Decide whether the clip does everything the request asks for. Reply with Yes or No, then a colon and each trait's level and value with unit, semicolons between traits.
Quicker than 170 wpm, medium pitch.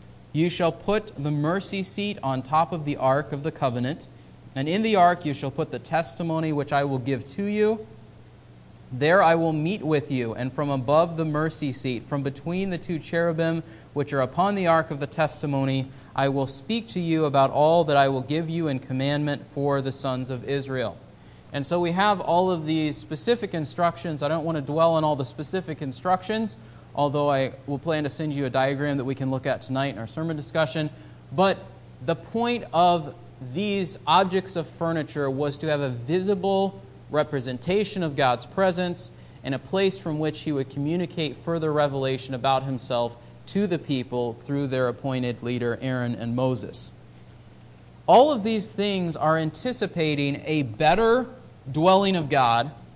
Yes: average, 180 wpm; medium, 150 Hz